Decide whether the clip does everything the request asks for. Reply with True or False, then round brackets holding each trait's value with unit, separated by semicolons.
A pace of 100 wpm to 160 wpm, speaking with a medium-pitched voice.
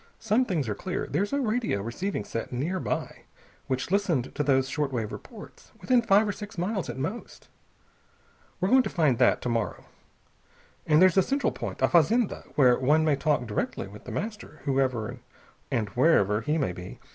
False (180 wpm; 150 Hz)